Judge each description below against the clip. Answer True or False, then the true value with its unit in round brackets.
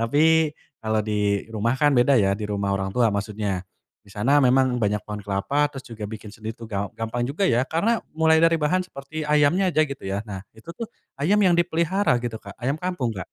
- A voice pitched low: True (125 Hz)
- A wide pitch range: True (6.9 semitones)